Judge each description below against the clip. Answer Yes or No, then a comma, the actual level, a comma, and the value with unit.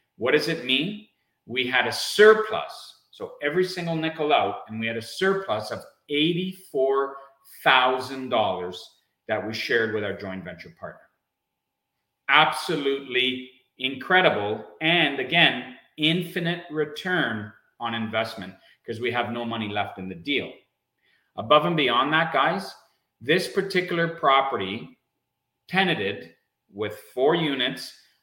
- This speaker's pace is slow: Yes, slow, 120 wpm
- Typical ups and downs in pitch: No, wide, 7.1 semitones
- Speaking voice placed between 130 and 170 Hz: Yes, low, 135 Hz